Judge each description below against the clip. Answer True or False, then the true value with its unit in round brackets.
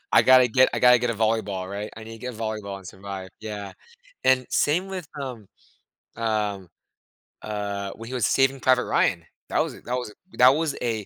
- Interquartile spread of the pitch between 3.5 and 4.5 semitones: True (3.8 semitones)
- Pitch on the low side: True (115 Hz)